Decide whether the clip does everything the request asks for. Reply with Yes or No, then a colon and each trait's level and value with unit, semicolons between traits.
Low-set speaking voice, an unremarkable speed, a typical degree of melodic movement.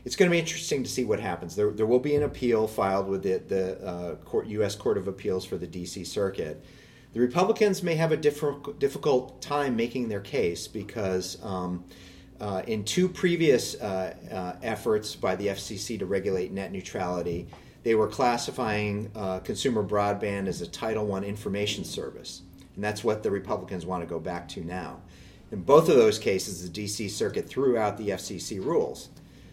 Yes: low, 105 Hz; average, 185 wpm; average, 5.0 semitones